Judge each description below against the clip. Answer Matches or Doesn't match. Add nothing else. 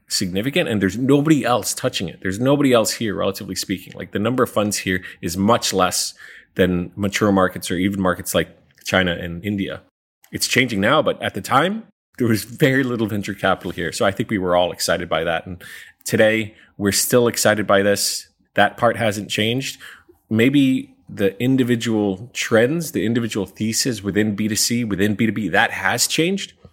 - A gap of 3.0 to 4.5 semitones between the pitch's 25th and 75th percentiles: Matches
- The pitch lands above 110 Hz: Doesn't match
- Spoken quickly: Doesn't match